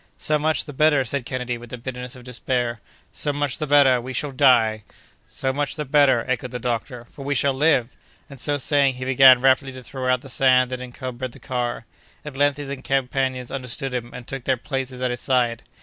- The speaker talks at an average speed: No, fast, 210 wpm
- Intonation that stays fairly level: Yes, narrow, 1.9 semitones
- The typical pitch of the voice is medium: No, low, 130 Hz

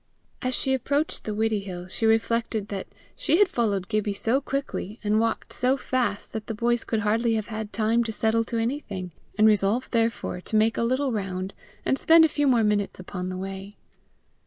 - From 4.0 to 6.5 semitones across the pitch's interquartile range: No, average, 2.8 semitones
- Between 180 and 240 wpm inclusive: Yes, average, 195 wpm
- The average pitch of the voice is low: No, high, 220 Hz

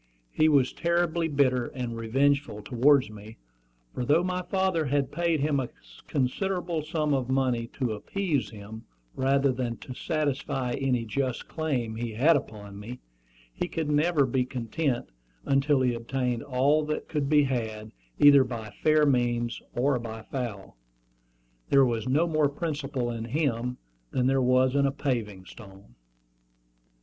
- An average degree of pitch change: Yes, average, 3.8 semitones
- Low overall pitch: Yes, low, 130 Hz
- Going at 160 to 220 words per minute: No, average, 150 wpm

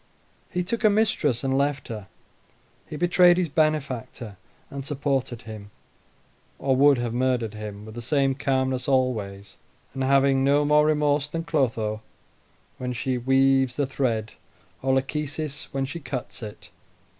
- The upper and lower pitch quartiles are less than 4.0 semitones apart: Yes, average, 3.2 semitones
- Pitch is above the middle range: No, low, 135 Hz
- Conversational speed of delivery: Yes, average, 145 wpm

